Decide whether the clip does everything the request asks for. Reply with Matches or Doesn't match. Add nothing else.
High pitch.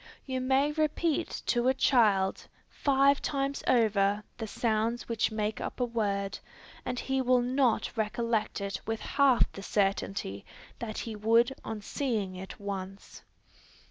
Matches